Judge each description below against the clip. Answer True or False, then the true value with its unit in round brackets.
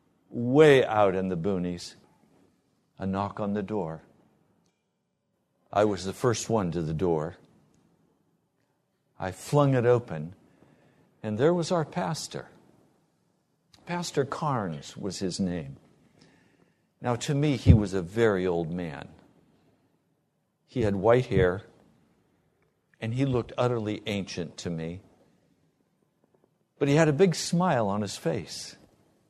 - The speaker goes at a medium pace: False (125 wpm)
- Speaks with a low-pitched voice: True (110 Hz)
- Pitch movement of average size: False (7.8 semitones)